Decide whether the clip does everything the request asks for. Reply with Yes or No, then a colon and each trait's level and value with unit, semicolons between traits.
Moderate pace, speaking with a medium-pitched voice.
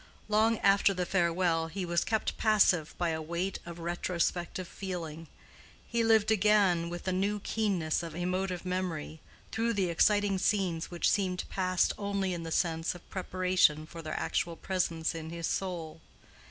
Yes: average, 160 wpm; medium, 180 Hz